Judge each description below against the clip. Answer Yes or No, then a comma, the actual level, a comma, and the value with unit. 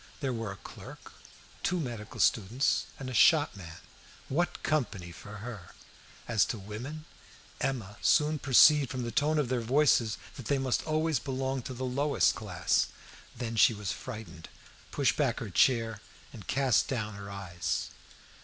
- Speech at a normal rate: Yes, average, 160 wpm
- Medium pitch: No, low, 120 Hz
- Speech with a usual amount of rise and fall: Yes, average, 4.6 semitones